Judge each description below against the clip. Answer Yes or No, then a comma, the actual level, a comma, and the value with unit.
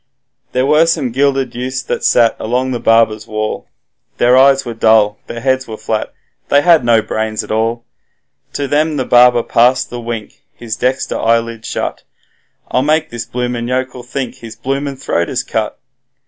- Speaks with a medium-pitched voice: No, low, 125 Hz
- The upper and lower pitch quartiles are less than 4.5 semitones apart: Yes, narrow, 2.6 semitones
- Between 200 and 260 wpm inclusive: No, average, 175 wpm